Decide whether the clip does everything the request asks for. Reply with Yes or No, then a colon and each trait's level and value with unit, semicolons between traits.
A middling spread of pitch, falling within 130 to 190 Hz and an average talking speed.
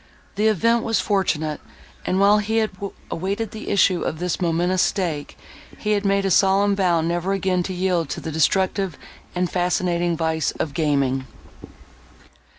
Yes: average, 3.1 semitones; medium, 185 Hz; average, 155 wpm